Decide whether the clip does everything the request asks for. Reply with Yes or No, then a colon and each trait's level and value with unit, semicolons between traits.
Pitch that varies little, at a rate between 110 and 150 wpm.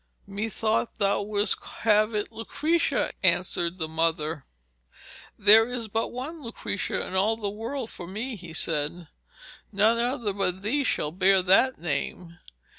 No: average, 4.2 semitones; average, 140 wpm